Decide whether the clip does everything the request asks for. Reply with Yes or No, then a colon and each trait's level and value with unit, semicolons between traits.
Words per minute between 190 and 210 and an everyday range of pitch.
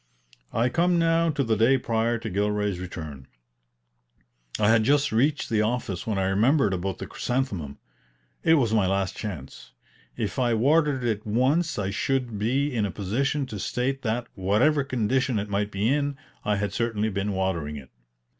No: average, 175 wpm; average, 5.0 semitones